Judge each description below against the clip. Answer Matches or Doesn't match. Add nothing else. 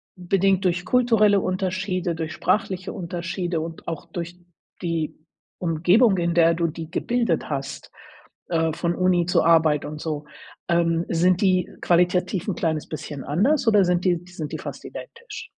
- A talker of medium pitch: Matches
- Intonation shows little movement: Matches